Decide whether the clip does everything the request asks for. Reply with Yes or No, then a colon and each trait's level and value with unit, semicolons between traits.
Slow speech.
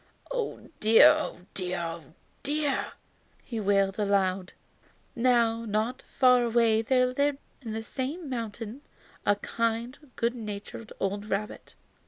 Yes: slow, 125 wpm